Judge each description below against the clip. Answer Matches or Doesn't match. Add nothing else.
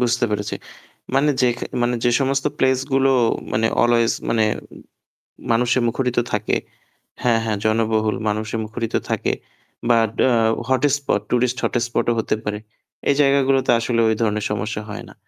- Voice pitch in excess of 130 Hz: Doesn't match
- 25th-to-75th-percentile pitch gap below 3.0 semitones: Matches